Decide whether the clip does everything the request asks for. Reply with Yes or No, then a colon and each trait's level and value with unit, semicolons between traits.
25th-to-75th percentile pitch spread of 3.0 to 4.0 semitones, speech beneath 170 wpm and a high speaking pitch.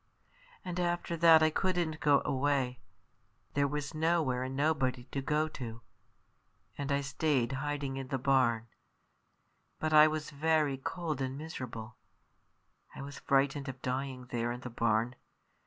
No: average, 3.3 semitones; average, 145 wpm; medium, 140 Hz